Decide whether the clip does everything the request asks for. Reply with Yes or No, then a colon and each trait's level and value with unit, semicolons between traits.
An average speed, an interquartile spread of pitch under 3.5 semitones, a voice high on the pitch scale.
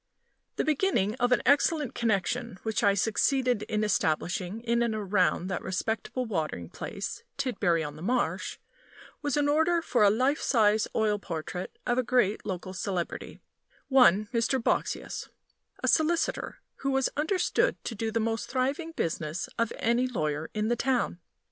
No: average, 155 wpm; average, 4.9 semitones; high, 225 Hz